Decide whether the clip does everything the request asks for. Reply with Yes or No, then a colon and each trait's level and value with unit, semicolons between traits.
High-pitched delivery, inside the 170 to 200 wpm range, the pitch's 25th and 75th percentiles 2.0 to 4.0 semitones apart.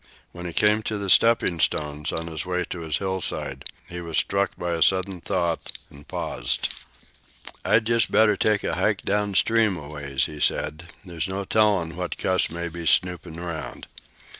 No: very low, 90 Hz; average, 175 wpm; average, 3.4 semitones